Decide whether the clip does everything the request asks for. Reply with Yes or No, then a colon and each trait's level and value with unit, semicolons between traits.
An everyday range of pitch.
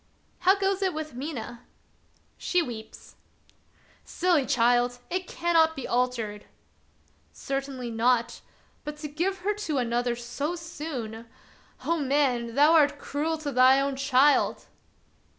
Yes: average, 4.8 semitones